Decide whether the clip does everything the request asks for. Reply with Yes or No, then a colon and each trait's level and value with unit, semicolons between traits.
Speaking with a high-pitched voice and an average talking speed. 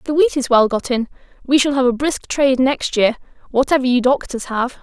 No: very high, 260 Hz; fast, 235 wpm